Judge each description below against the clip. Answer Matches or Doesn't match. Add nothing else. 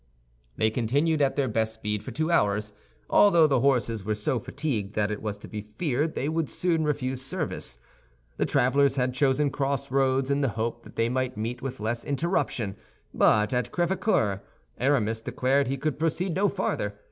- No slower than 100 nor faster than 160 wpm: Doesn't match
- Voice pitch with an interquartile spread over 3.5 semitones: Matches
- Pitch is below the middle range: Matches